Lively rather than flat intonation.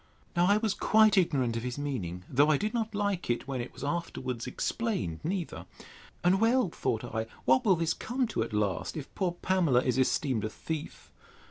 Yes: wide, 8.1 semitones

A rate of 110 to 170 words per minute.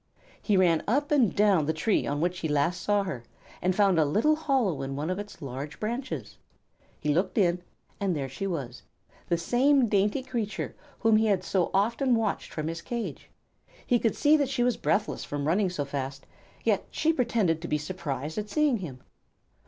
No: average, 195 wpm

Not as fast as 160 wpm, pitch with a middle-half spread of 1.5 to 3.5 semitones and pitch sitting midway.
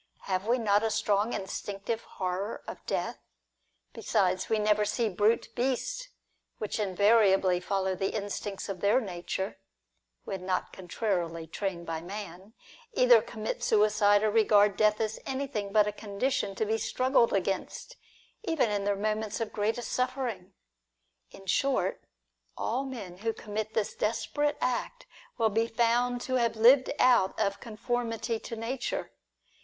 No: average, 145 wpm; average, 2.9 semitones; high, 215 Hz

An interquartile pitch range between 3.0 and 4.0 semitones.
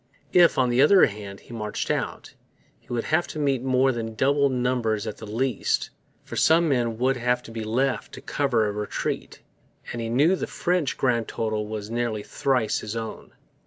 Yes: average, 3.4 semitones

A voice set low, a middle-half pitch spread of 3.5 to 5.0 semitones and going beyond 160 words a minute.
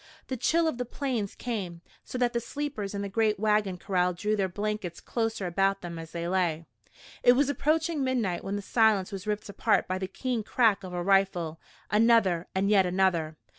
No: high, 200 Hz; average, 4.1 semitones; average, 200 wpm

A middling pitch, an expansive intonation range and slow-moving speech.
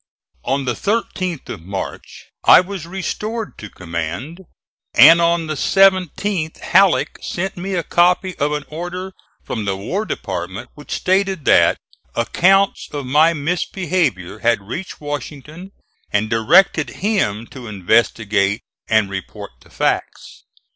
Yes: medium, 155 Hz; wide, 9.0 semitones; slow, 130 wpm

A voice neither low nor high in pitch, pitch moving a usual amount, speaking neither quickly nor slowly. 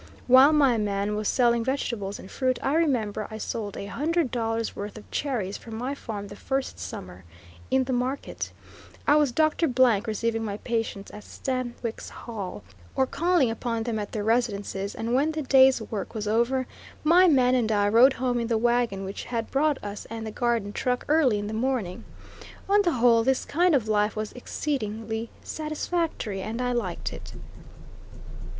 No: high, 235 Hz; average, 3.7 semitones; average, 180 wpm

